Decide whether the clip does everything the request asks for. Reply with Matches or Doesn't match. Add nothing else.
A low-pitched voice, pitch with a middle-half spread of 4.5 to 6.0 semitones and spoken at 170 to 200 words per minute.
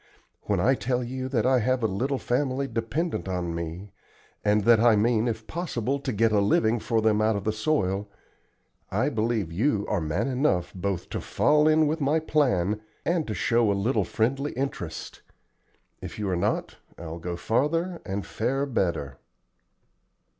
Matches